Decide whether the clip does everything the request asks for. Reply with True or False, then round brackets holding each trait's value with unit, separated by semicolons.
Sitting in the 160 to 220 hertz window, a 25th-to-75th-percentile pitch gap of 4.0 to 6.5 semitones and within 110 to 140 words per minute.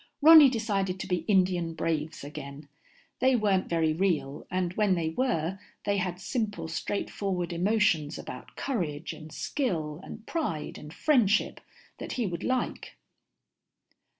True (185 Hz; 4.9 semitones; 135 wpm)